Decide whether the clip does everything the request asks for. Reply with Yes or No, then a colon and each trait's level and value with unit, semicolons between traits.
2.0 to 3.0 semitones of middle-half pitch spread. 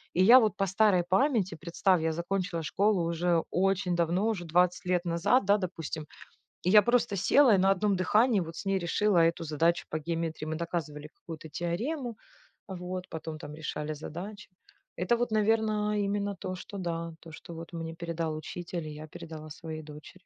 No: average, 3.5 semitones